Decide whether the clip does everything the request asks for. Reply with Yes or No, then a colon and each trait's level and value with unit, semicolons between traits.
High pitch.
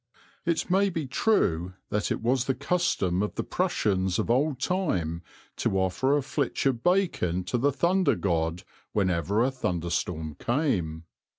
No: low, 115 Hz